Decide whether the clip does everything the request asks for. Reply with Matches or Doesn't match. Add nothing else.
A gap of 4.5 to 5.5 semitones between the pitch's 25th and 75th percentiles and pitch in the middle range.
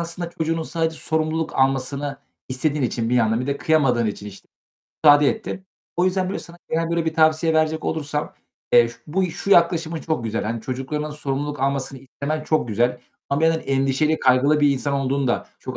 Doesn't match